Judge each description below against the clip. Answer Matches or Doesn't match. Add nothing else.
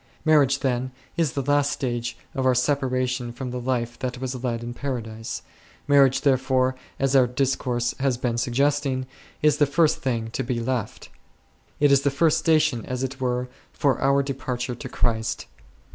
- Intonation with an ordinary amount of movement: Doesn't match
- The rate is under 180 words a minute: Matches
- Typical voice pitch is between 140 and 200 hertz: Doesn't match